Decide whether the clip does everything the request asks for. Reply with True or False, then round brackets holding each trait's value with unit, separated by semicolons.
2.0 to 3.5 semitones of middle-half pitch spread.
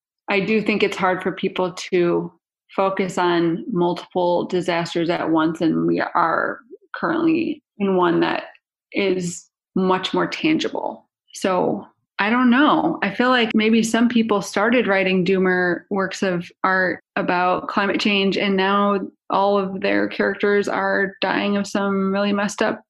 True (2.4 semitones)